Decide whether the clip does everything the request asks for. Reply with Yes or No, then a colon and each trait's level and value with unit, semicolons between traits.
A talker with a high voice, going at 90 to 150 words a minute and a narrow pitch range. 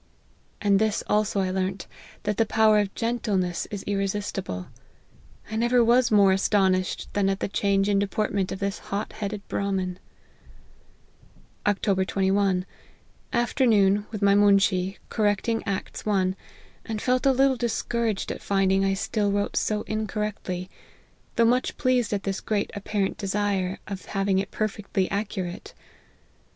Yes: high, 200 Hz; average, 145 wpm; narrow, 1.9 semitones